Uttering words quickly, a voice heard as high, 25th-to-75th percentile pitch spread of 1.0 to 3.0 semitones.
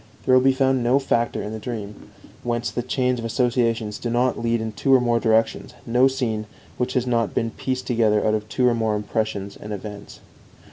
No: fast, 215 wpm; low, 115 Hz; narrow, 2.6 semitones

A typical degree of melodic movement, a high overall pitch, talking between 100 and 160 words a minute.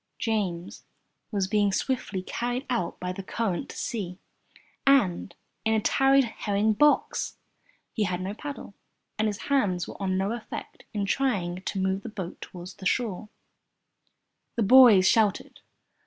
Yes: average, 4.0 semitones; high, 205 Hz; average, 150 wpm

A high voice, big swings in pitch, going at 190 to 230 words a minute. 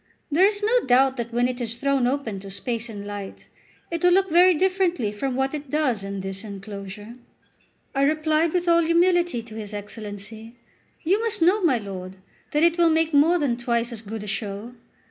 Yes: very high, 255 Hz; wide, 7.9 semitones; average, 200 wpm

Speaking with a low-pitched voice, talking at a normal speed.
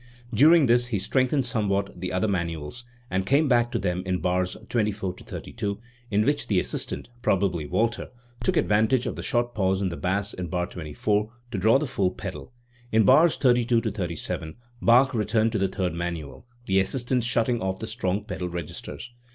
Yes: low, 105 Hz; average, 180 wpm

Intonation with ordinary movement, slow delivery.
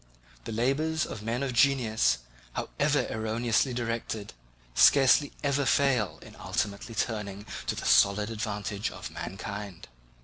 Yes: average, 4.4 semitones; slow, 125 wpm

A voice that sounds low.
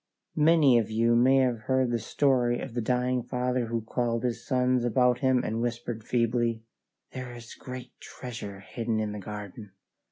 Yes: low, 120 Hz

